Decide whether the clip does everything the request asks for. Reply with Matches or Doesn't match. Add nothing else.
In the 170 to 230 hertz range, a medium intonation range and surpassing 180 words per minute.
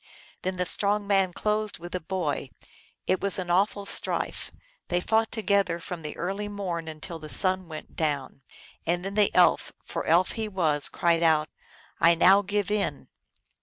Doesn't match